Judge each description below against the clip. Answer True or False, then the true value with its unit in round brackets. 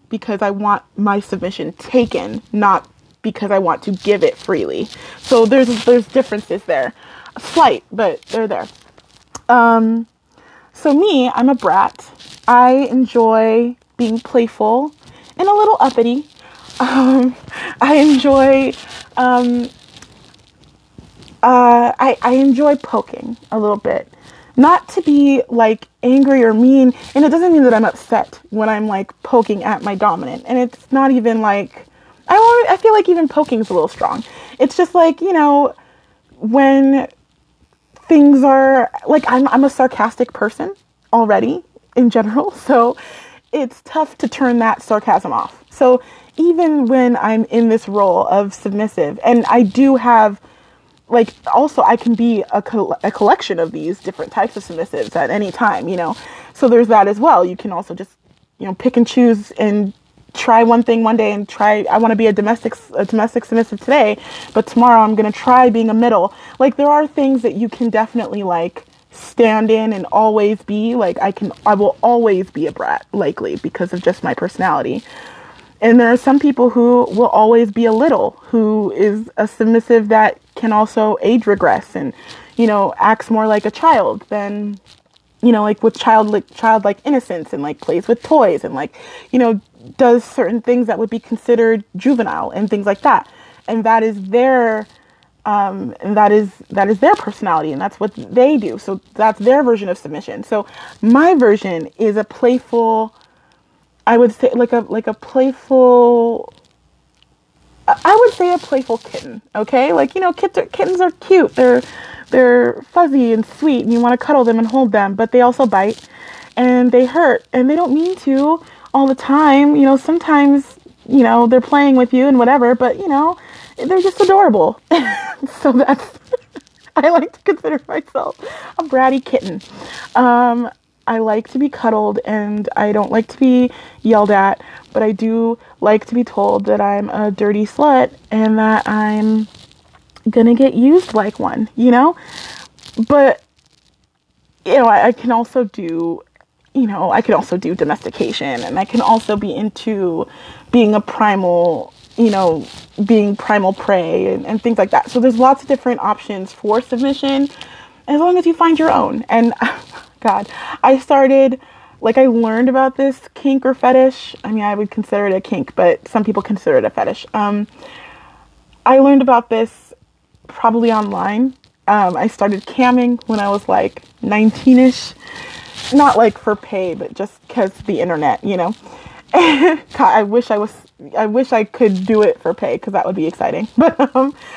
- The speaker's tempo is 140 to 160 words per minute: False (175 wpm)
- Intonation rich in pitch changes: False (3.8 semitones)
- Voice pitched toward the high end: True (240 Hz)